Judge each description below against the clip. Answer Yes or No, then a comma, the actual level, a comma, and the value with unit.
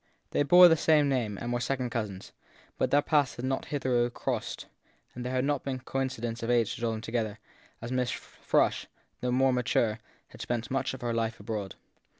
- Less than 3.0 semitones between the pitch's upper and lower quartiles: Yes, narrow, 2.5 semitones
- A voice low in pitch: Yes, low, 125 Hz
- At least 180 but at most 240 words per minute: Yes, average, 195 wpm